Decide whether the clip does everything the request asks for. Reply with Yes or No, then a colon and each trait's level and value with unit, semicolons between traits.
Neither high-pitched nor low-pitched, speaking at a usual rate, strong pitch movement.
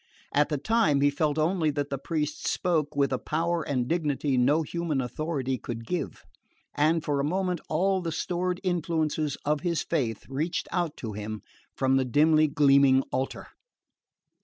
No: medium, 150 Hz; average, 165 wpm; average, 3.4 semitones